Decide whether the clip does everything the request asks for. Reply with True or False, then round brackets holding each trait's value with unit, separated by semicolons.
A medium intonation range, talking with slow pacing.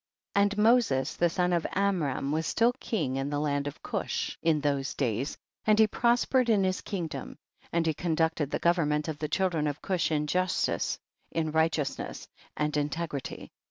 False (4.1 semitones; 180 wpm)